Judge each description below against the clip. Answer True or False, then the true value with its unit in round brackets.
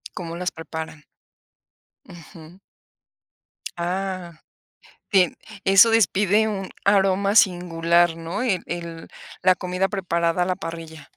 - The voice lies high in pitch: False (180 Hz)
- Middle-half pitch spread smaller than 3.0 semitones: True (2.5 semitones)